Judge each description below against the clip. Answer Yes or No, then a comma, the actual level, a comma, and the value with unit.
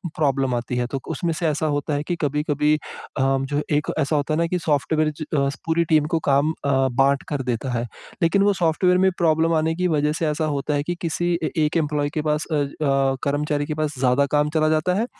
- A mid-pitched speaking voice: Yes, medium, 150 Hz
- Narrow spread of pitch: Yes, narrow, 2.3 semitones